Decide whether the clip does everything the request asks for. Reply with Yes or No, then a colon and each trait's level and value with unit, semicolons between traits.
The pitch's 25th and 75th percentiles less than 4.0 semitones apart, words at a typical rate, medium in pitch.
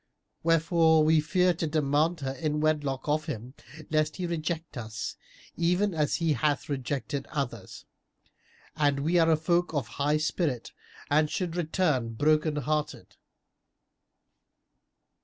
No: narrow, 2.5 semitones; slow, 130 wpm; medium, 155 Hz